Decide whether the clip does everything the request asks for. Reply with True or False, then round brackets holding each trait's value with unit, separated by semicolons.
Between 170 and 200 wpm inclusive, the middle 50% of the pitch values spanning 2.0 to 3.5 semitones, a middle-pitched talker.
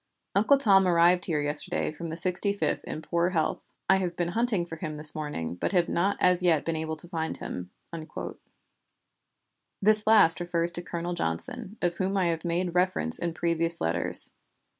True (180 wpm; 2.5 semitones; 175 Hz)